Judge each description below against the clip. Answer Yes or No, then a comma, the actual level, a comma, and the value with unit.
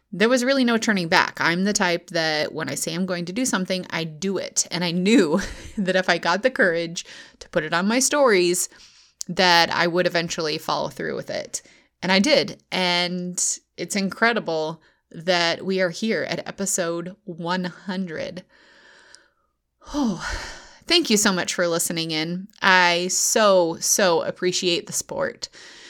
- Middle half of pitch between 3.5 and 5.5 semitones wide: No, average, 2.9 semitones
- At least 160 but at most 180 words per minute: Yes, average, 165 wpm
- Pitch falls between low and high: Yes, medium, 180 Hz